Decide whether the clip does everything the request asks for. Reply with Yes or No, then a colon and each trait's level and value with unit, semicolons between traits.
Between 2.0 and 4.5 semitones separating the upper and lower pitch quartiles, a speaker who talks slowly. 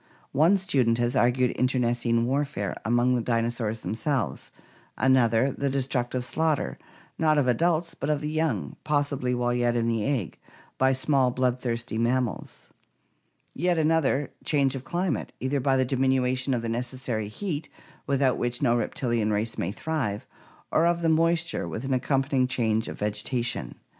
No: average, 3.4 semitones; average, 155 wpm